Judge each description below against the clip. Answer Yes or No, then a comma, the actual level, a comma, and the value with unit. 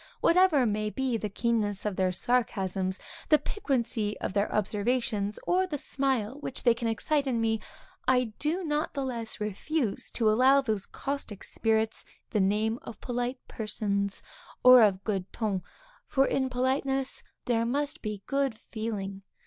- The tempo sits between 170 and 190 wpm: No, average, 155 wpm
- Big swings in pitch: No, average, 4.2 semitones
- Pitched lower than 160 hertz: No, high, 230 Hz